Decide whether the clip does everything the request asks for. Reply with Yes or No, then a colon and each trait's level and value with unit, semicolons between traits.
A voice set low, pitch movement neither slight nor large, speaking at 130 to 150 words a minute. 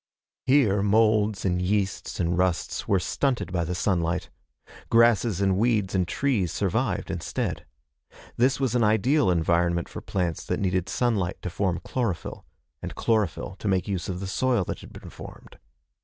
No: very low, 95 Hz; average, 3.9 semitones; average, 160 wpm